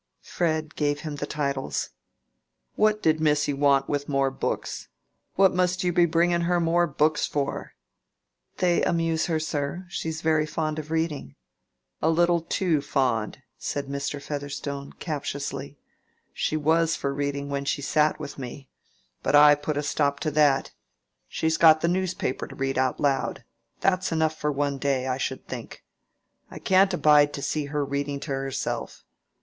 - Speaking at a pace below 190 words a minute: Yes, average, 165 wpm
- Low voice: No, medium, 150 Hz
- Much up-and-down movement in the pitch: No, narrow, 2.5 semitones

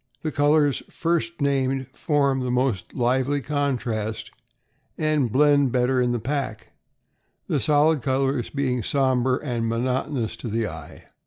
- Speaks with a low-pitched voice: Yes, low, 130 Hz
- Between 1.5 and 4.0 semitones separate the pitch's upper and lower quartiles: Yes, average, 3.0 semitones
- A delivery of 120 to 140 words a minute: Yes, slow, 135 wpm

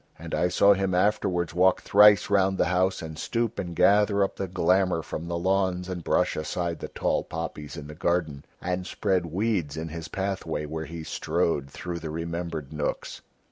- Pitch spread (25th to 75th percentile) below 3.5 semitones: Yes, average, 2.9 semitones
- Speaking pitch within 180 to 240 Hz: No, very low, 90 Hz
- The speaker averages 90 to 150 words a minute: No, average, 185 wpm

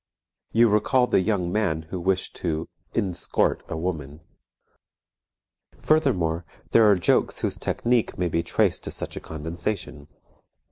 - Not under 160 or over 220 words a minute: No, slow, 135 wpm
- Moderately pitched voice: No, very low, 90 Hz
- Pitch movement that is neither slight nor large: Yes, average, 4.8 semitones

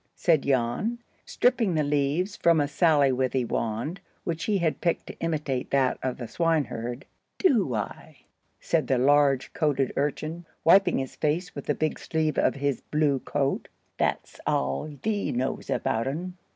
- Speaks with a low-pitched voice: No, medium, 145 Hz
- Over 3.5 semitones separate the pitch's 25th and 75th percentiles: Yes, average, 4.0 semitones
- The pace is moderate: Yes, average, 155 wpm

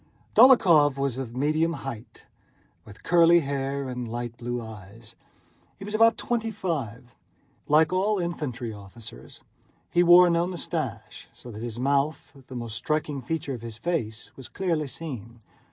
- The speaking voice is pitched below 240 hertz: Yes, medium, 140 Hz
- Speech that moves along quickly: No, average, 150 wpm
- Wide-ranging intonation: Yes, wide, 6.1 semitones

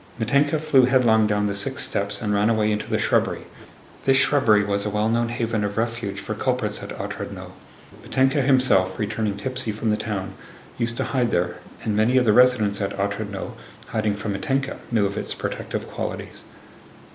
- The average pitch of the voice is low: Yes, low, 110 Hz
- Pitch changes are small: No, average, 3.4 semitones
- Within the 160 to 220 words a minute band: Yes, average, 180 wpm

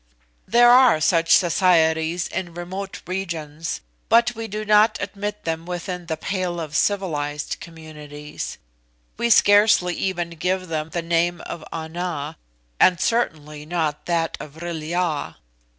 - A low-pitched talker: No, medium, 175 Hz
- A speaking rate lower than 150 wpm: Yes, slow, 135 wpm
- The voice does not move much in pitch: No, average, 3.1 semitones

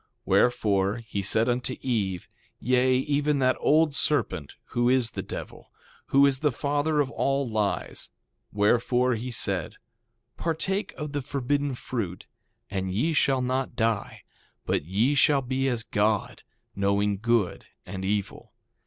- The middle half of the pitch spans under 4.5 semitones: No, average, 5.1 semitones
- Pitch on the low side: Yes, low, 125 Hz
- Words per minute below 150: Yes, average, 140 wpm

